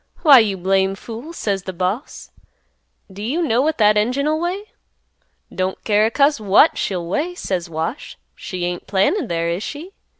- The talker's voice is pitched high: Yes, high, 210 Hz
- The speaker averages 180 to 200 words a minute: No, average, 170 wpm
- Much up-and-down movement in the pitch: Yes, wide, 7.5 semitones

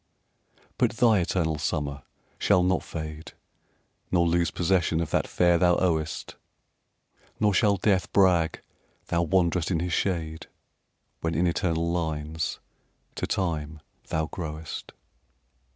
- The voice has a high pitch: No, very low, 85 Hz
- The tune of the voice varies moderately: No, narrow, 2.3 semitones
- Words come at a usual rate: No, slow, 120 wpm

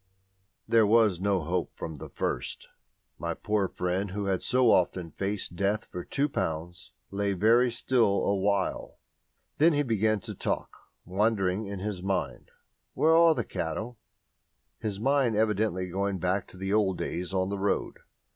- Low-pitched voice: Yes, low, 100 Hz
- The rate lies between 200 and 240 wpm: No, average, 155 wpm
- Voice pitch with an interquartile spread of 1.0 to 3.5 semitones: Yes, average, 3.1 semitones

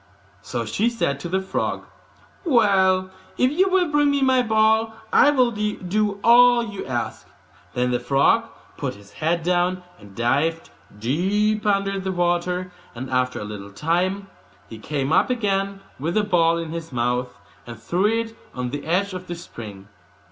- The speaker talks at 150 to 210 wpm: Yes, average, 170 wpm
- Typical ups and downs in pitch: No, wide, 7.7 semitones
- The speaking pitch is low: No, medium, 180 Hz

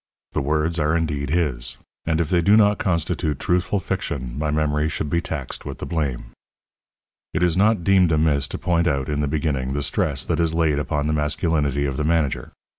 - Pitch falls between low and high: No, very low, 75 Hz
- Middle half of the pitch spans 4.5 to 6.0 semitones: No, average, 2.7 semitones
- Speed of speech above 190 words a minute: Yes, average, 200 wpm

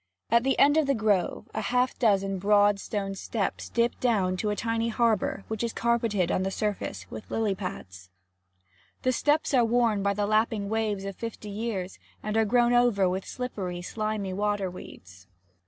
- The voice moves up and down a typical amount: Yes, average, 3.1 semitones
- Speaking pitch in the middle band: No, high, 210 Hz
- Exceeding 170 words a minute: Yes, average, 180 wpm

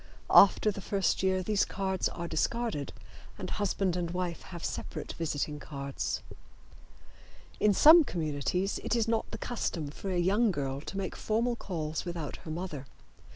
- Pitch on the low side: No, medium, 185 Hz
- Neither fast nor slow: Yes, average, 155 wpm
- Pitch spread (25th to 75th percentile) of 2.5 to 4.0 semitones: No, average, 4.6 semitones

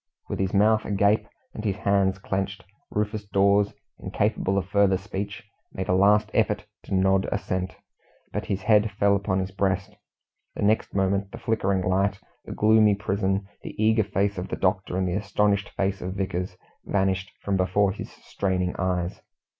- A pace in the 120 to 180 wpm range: Yes, average, 170 wpm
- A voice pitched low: Yes, low, 100 Hz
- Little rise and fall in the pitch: Yes, narrow, 1.3 semitones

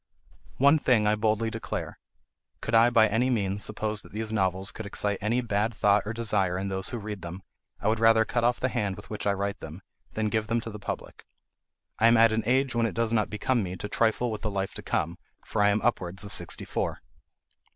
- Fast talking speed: Yes, fast, 235 wpm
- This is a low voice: Yes, low, 110 Hz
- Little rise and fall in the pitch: Yes, narrow, 2.2 semitones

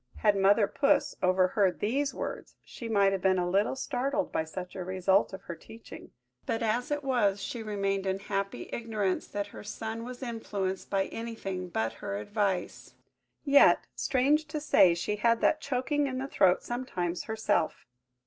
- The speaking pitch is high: Yes, high, 205 Hz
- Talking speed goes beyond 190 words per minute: No, average, 170 wpm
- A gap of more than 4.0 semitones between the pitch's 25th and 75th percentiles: Yes, average, 4.4 semitones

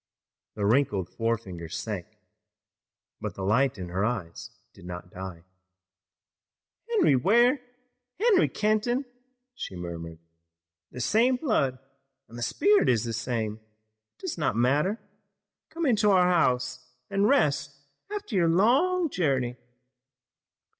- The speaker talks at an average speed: No, slow, 120 wpm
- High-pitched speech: No, low, 135 Hz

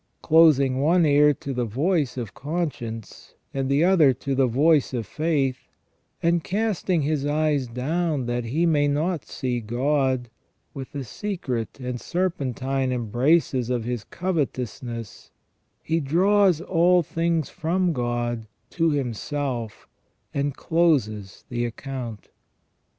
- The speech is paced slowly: Yes, slow, 130 wpm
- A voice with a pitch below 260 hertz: Yes, medium, 140 Hz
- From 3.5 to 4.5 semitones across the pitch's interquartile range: No, average, 5.0 semitones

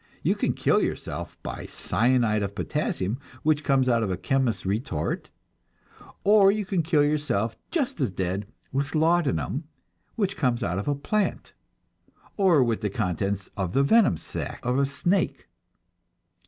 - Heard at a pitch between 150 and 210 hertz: No, low, 130 Hz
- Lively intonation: Yes, wide, 7.6 semitones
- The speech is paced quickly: No, average, 155 wpm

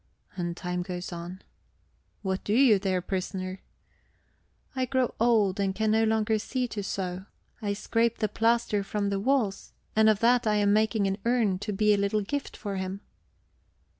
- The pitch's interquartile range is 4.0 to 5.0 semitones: No, average, 2.7 semitones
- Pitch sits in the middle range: No, high, 205 Hz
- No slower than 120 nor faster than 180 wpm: Yes, average, 175 wpm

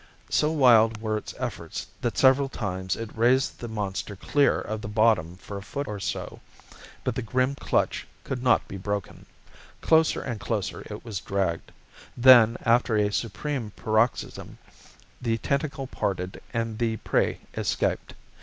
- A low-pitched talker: Yes, low, 115 Hz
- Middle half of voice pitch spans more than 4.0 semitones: No, average, 3.7 semitones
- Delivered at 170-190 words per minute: No, average, 155 wpm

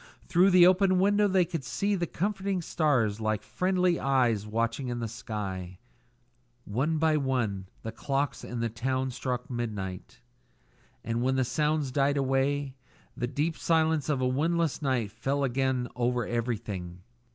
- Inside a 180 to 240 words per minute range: No, average, 150 wpm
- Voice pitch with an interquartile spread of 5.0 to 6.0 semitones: Yes, wide, 5.4 semitones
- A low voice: Yes, low, 130 Hz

